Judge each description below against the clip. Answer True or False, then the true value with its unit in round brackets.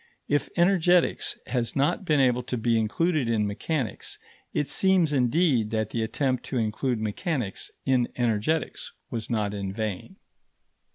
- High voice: False (125 Hz)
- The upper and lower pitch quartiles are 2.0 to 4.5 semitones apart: False (5.6 semitones)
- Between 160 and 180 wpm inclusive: False (140 wpm)